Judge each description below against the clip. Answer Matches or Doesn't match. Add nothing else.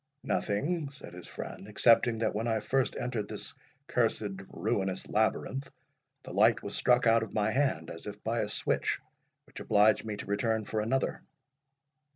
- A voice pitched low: Matches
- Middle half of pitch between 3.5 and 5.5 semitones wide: Doesn't match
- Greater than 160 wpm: Matches